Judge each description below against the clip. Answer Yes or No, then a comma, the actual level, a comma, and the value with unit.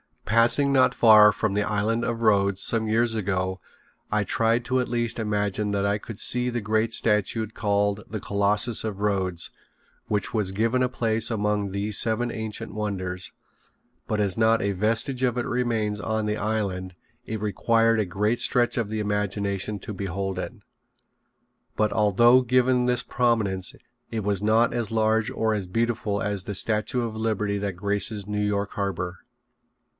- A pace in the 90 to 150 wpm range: No, average, 170 wpm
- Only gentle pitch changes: Yes, narrow, 2.1 semitones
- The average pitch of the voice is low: Yes, low, 105 Hz